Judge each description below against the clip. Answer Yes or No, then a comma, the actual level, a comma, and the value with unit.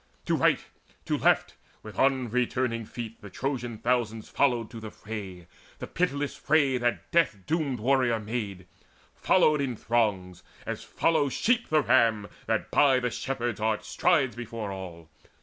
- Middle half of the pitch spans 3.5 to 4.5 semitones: Yes, average, 4.0 semitones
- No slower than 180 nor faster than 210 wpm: No, average, 150 wpm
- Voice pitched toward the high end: No, low, 120 Hz